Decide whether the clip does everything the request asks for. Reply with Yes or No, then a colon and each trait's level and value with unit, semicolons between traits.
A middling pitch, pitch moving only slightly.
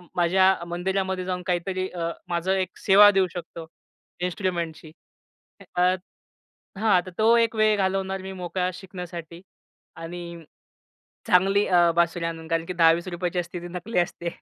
Yes: medium, 180 Hz; narrow, 1.8 semitones